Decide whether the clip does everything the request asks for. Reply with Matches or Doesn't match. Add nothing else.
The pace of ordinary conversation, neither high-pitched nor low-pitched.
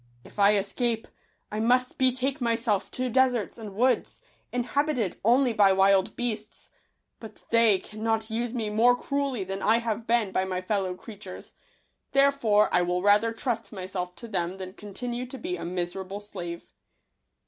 Doesn't match